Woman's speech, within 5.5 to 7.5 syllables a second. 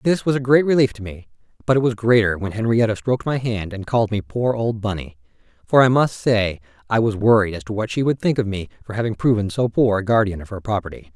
No: male; 6.1 syllables/s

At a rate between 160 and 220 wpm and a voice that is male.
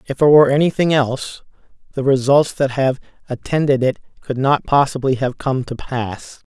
Yes: average, 165 wpm; male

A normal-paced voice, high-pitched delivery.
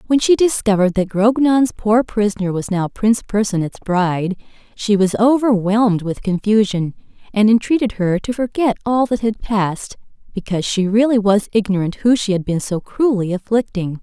Yes: average, 165 wpm; high, 210 Hz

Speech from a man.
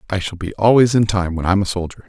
Yes: male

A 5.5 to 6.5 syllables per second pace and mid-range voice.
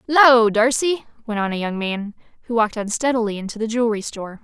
No: 6.2 syllables/s; high, 225 Hz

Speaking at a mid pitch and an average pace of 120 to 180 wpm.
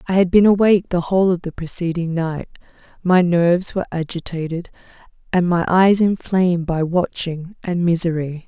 Yes: medium, 175 Hz; average, 155 wpm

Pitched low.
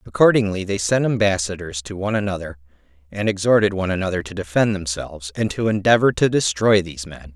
Yes: very low, 95 Hz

